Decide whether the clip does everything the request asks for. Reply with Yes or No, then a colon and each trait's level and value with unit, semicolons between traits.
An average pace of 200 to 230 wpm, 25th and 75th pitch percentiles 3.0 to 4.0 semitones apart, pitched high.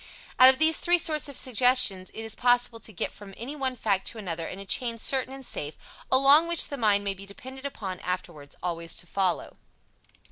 No: fast, 205 wpm; wide, 5.6 semitones; high, 230 Hz